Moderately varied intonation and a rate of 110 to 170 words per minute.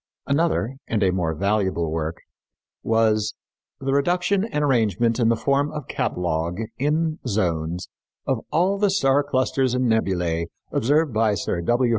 No: wide, 7.5 semitones; average, 145 wpm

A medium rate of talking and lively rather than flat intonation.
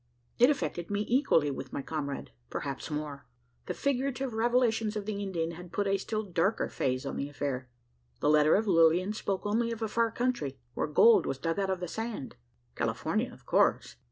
Yes: average, 190 wpm; wide, 6.8 semitones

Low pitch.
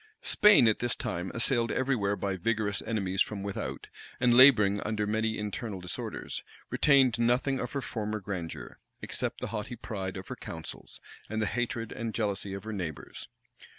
Yes: low, 110 Hz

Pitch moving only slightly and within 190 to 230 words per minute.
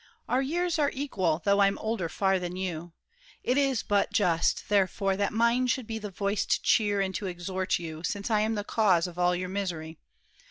No: average, 3.7 semitones; fast, 205 wpm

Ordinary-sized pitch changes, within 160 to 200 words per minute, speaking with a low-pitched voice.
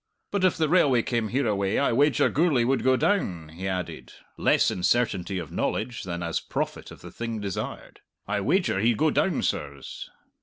No: wide, 6.8 semitones; average, 185 wpm; low, 115 Hz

